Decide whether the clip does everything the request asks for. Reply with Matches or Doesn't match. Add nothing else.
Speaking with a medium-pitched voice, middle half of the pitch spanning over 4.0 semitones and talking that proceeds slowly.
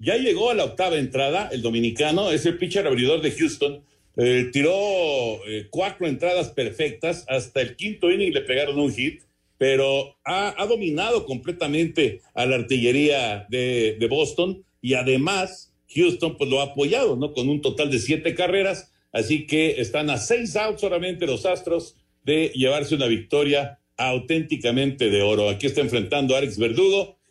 Doesn't match